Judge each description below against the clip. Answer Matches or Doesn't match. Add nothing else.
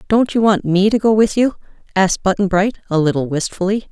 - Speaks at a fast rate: Matches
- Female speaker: Matches